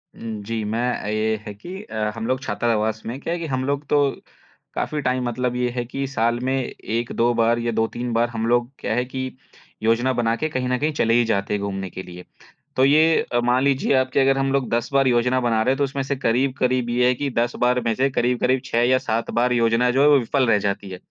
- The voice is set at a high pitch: No, low, 120 Hz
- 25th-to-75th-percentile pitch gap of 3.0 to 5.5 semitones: No, narrow, 2.4 semitones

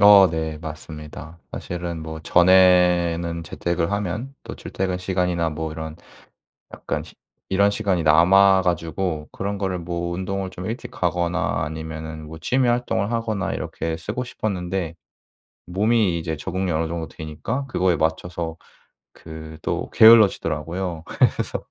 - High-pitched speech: No, very low, 85 Hz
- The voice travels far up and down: No, average, 3.2 semitones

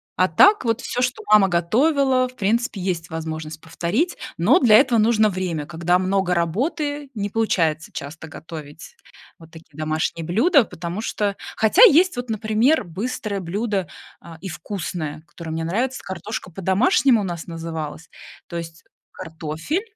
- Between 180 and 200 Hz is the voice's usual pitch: Yes, medium, 185 Hz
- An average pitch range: No, wide, 6.2 semitones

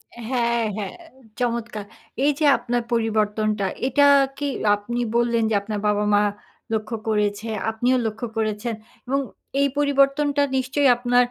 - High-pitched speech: Yes, high, 235 Hz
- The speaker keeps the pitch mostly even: No, average, 3.2 semitones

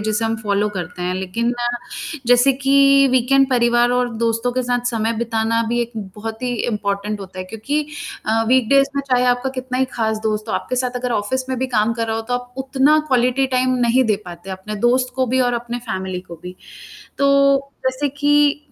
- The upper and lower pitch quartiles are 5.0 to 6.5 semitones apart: No, average, 3.0 semitones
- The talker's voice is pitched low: No, high, 240 Hz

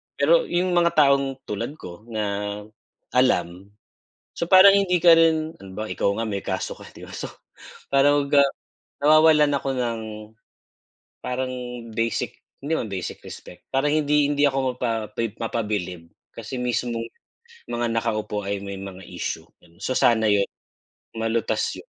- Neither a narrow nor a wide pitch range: No, wide, 5.7 semitones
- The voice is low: Yes, low, 120 Hz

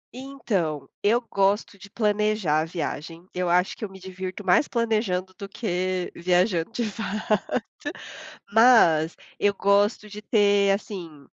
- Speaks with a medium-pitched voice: No, high, 200 Hz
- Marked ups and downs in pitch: No, average, 3.0 semitones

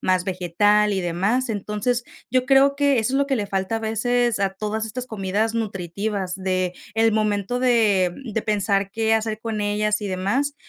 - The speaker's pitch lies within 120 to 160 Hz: No, high, 215 Hz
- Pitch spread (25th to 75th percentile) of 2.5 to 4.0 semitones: Yes, average, 2.9 semitones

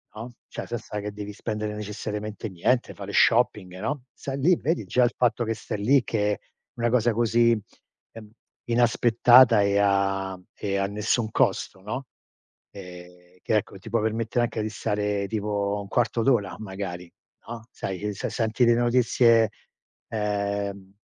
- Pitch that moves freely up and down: No, average, 2.7 semitones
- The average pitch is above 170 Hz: No, low, 105 Hz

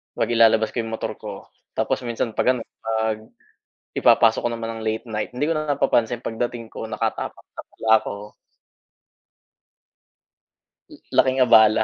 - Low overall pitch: Yes, low, 115 Hz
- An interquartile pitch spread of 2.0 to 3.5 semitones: No, narrow, 1.4 semitones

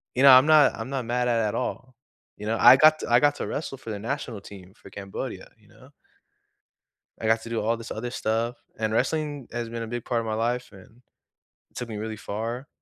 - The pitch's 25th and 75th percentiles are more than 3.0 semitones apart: No, average, 2.7 semitones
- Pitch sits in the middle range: No, low, 115 Hz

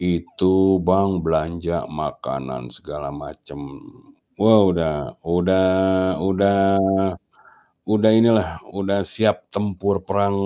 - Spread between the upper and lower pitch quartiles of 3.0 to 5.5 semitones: Yes, average, 3.6 semitones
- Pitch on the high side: No, very low, 95 Hz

